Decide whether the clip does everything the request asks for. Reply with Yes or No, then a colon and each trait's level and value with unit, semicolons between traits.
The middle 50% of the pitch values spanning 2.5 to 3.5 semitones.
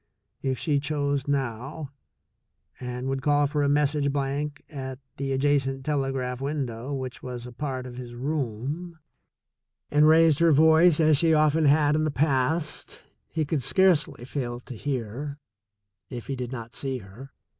Yes: average, 2.8 semitones